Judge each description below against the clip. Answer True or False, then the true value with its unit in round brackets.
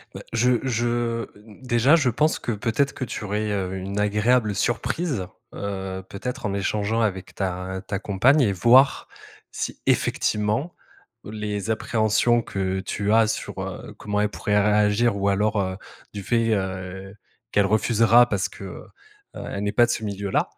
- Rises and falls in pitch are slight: False (3.0 semitones)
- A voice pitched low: True (105 Hz)